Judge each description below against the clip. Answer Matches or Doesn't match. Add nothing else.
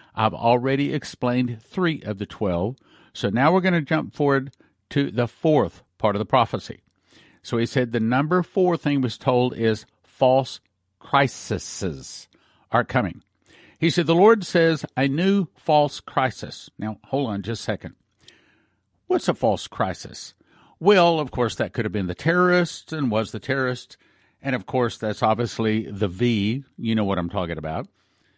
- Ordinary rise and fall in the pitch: Doesn't match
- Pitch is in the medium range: Doesn't match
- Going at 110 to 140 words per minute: Doesn't match